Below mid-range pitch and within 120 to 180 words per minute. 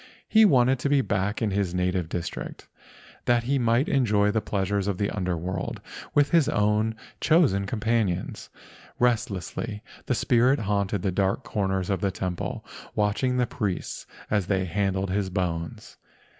Yes: low, 105 Hz; average, 155 wpm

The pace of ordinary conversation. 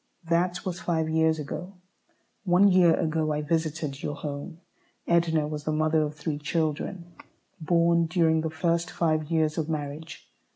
Yes: average, 155 wpm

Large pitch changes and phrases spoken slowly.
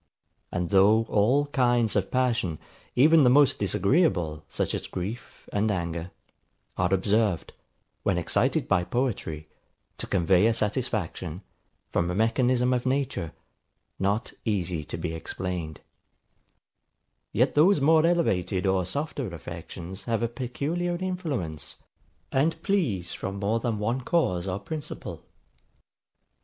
Yes: wide, 6.4 semitones; slow, 125 wpm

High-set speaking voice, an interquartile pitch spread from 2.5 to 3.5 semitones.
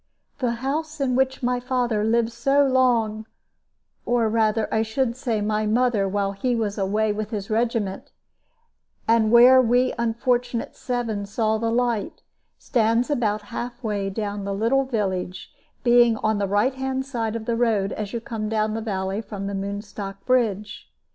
Yes: high, 225 Hz; average, 2.8 semitones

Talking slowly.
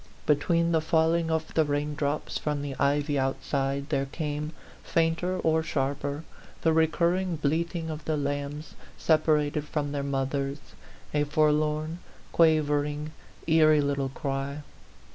Yes: slow, 125 wpm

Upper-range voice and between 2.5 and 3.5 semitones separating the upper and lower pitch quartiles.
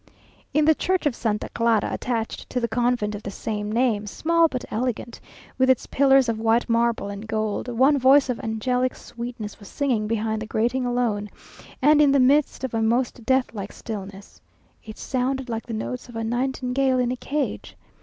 Yes: high, 240 Hz; average, 2.9 semitones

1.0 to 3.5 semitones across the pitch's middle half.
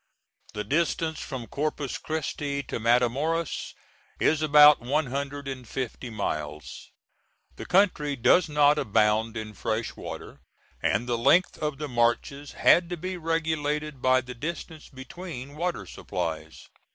No: average, 4.6 semitones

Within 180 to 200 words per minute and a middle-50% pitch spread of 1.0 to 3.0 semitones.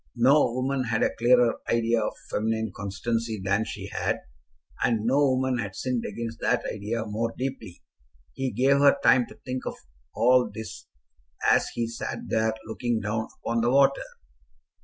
No: average, 160 wpm; narrow, 2.5 semitones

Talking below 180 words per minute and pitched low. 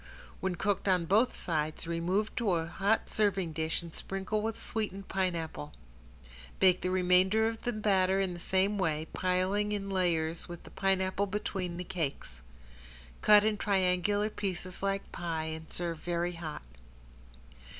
No: average, 150 wpm; medium, 185 Hz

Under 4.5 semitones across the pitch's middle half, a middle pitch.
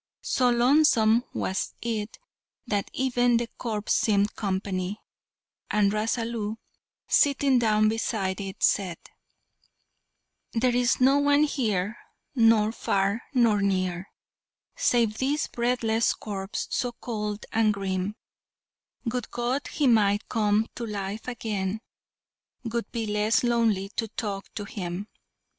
No: average, 3.0 semitones; high, 220 Hz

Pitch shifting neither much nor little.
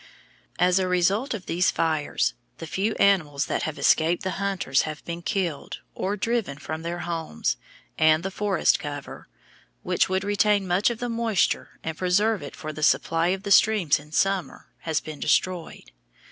Yes: average, 4.0 semitones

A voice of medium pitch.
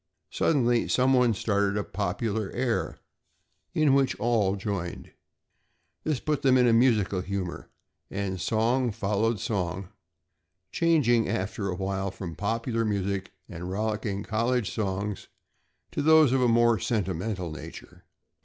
No: low, 110 Hz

